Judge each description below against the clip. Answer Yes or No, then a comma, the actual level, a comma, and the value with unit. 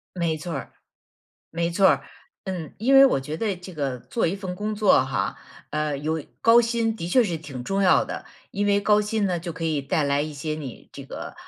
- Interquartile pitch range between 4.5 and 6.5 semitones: Yes, average, 5.2 semitones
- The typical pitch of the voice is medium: Yes, medium, 170 Hz